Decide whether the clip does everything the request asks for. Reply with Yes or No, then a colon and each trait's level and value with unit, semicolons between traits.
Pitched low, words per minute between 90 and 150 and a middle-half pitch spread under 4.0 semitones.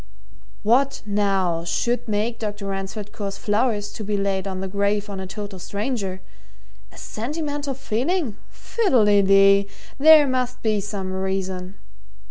No: high, 205 Hz; average, 140 wpm; average, 3.6 semitones